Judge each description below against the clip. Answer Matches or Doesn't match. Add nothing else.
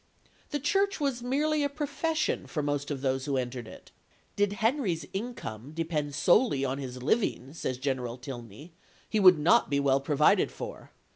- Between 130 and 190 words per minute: Matches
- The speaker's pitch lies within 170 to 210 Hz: Doesn't match